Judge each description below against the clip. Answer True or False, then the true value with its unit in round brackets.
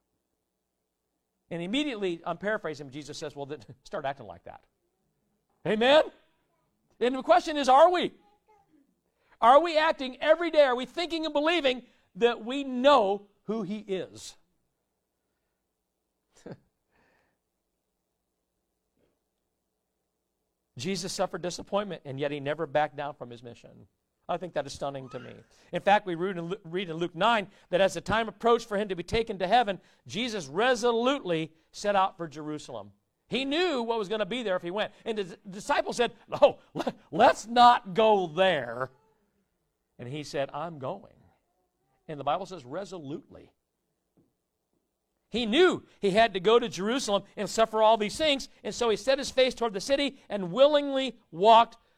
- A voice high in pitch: True (210 Hz)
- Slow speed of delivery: False (155 wpm)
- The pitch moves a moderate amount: False (6.6 semitones)